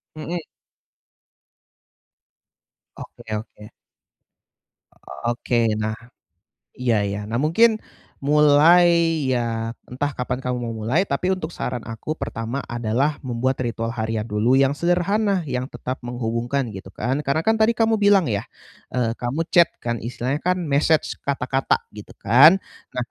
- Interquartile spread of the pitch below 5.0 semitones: No, wide, 5.4 semitones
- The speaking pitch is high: No, low, 130 Hz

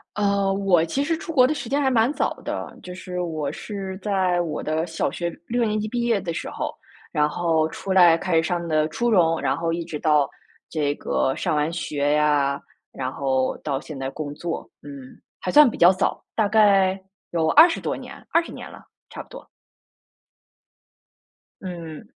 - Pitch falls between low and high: Yes, medium, 175 Hz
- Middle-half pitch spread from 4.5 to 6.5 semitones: Yes, average, 5.0 semitones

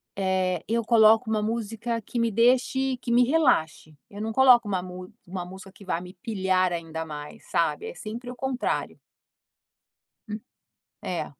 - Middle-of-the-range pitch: No, high, 215 Hz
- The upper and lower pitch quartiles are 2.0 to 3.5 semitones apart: No, average, 4.4 semitones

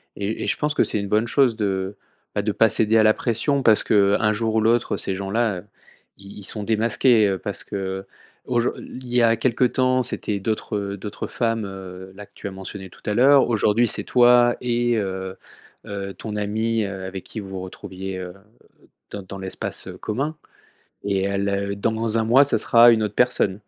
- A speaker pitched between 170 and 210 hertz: No, low, 105 Hz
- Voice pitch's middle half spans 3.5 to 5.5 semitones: No, average, 3.0 semitones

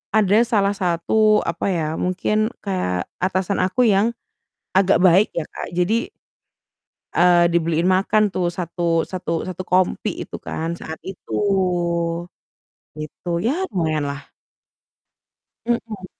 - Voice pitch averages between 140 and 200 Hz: Yes, medium, 185 Hz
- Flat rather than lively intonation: No, average, 3.3 semitones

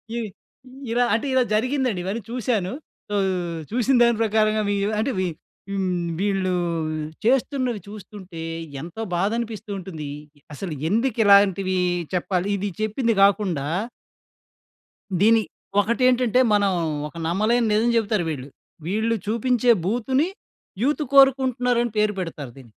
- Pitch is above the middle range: Yes, high, 215 Hz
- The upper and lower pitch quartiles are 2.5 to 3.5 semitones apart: No, average, 4.0 semitones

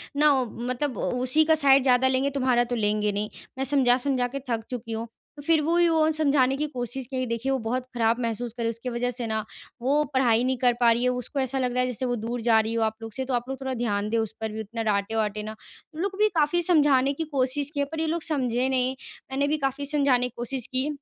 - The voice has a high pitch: Yes, very high, 250 Hz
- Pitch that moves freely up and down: No, average, 3.2 semitones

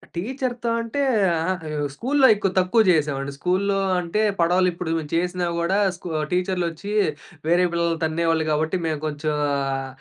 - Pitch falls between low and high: Yes, medium, 170 Hz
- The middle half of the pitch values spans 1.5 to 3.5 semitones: Yes, average, 2.9 semitones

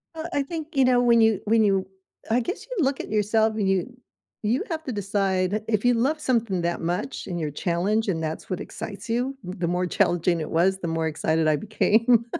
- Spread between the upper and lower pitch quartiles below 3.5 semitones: No, average, 5.3 semitones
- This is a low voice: No, high, 210 Hz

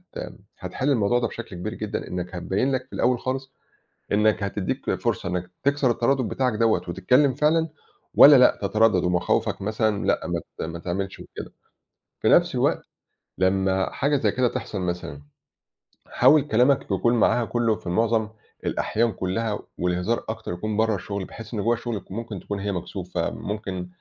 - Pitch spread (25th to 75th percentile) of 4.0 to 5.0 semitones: Yes, average, 4.4 semitones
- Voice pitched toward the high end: No, low, 110 Hz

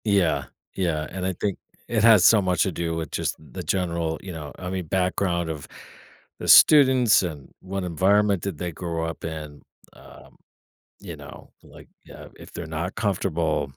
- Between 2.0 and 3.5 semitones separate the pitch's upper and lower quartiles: Yes, average, 3.2 semitones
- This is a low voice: Yes, very low, 90 Hz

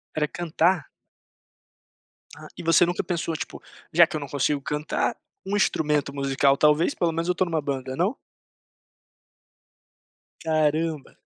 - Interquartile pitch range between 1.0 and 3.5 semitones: Yes, average, 2.8 semitones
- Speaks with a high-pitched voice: No, medium, 155 Hz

